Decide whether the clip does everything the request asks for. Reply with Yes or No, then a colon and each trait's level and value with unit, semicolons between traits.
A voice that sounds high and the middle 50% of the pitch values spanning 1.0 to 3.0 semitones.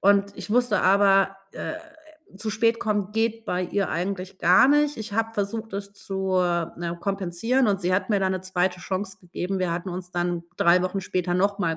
Yes: high, 195 Hz; narrow, 2.5 semitones